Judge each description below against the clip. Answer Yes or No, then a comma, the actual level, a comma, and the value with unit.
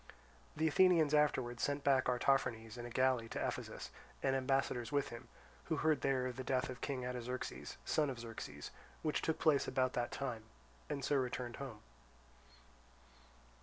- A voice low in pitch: Yes, low, 130 Hz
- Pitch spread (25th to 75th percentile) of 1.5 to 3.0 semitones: Yes, average, 2.7 semitones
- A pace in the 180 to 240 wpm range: No, average, 165 wpm